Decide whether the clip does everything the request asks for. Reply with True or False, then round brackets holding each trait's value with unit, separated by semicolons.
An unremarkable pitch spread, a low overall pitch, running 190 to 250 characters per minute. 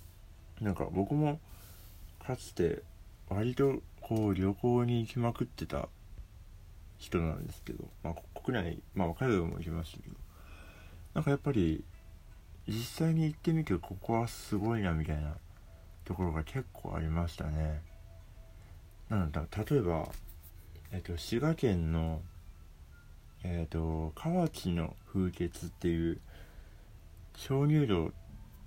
True (4.6 semitones; 90 Hz; 230 characters per minute)